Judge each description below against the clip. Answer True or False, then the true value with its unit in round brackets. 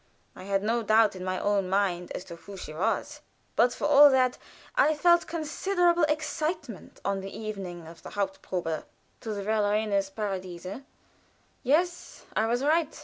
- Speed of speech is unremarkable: True (165 wpm)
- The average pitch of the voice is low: False (215 Hz)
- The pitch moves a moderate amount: False (7.4 semitones)